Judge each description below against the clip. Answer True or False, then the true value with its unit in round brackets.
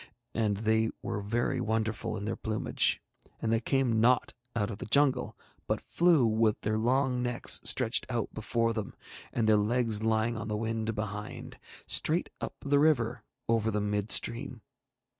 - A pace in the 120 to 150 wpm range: False (165 wpm)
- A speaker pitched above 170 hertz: False (115 Hz)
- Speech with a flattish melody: True (2.0 semitones)